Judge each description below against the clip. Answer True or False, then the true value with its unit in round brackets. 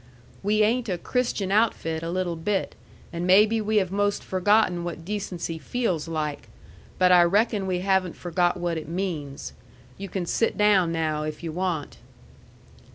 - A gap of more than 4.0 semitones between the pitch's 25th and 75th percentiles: False (3.6 semitones)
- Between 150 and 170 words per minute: True (160 wpm)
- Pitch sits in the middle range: True (180 Hz)